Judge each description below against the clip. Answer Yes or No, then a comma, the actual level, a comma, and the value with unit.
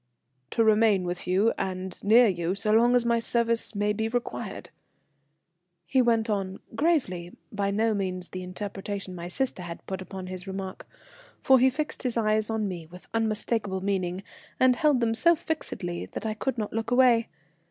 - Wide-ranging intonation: No, average, 3.8 semitones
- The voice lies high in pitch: Yes, high, 210 Hz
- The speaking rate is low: No, average, 175 wpm